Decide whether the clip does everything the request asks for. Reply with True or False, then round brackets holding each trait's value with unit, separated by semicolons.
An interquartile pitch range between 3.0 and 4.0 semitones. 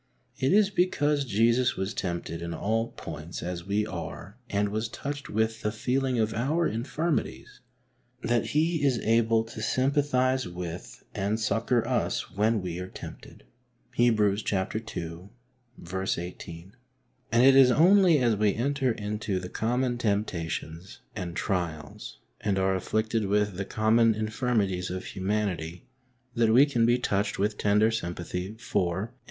False (4.4 semitones)